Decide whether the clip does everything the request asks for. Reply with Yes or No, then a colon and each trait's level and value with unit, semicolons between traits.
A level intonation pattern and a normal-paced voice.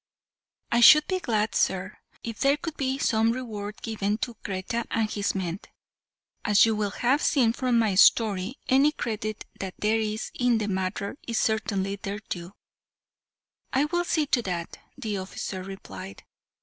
No: average, 3.7 semitones; average, 160 wpm